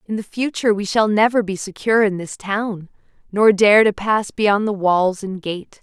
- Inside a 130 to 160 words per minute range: No, fast, 205 wpm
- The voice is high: Yes, high, 205 Hz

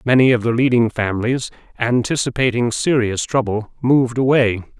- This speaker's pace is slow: Yes, slow, 125 wpm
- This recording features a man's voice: Yes, male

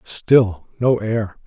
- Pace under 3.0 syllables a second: Yes, 2.5 syllables/s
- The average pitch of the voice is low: Yes, low, 110 Hz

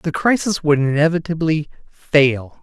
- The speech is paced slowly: Yes, slow, 115 wpm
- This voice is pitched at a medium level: Yes, medium, 155 Hz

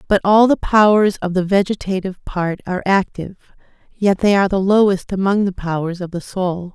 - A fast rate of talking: No, average, 185 wpm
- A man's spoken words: No, female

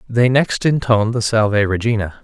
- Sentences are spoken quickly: No, average, 160 wpm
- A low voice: Yes, low, 115 Hz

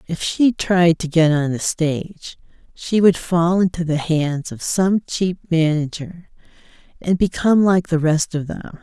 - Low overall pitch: No, medium, 170 Hz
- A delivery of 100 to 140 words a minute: No, average, 170 wpm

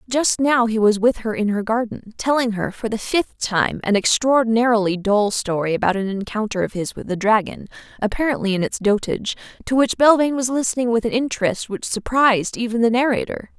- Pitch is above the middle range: Yes, high, 225 Hz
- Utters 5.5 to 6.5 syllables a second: Yes, 5.7 syllables/s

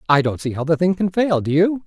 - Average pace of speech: No, fast, 320 wpm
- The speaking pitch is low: No, medium, 170 Hz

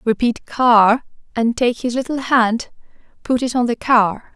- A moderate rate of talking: Yes, average, 165 wpm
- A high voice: Yes, high, 235 Hz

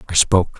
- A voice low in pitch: Yes, very low, 90 Hz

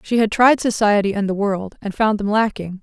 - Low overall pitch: No, high, 210 Hz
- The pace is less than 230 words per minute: No, fast, 235 wpm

